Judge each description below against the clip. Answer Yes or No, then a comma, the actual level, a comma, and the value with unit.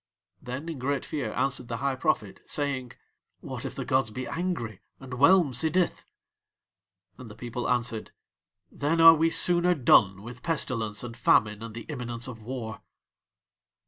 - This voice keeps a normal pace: Yes, average, 155 wpm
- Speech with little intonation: No, average, 4.4 semitones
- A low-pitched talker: Yes, low, 125 Hz